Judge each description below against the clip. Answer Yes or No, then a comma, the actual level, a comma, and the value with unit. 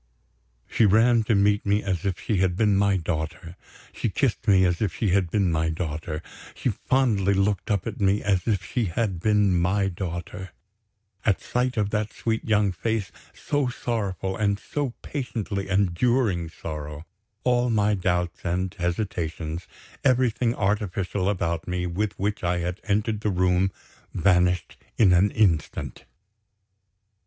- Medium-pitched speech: No, very low, 95 Hz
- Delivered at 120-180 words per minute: Yes, average, 155 wpm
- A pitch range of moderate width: Yes, average, 3.3 semitones